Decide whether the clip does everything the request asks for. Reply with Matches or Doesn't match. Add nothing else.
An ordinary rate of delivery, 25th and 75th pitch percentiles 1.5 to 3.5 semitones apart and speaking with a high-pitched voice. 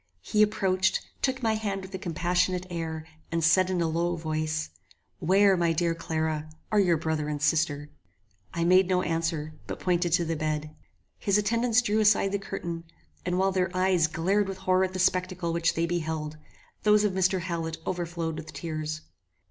Doesn't match